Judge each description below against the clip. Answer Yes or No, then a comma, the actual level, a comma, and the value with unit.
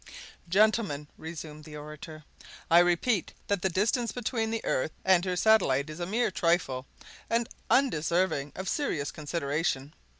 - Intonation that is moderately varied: No, wide, 6.1 semitones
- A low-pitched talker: No, medium, 175 Hz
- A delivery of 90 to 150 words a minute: Yes, average, 140 wpm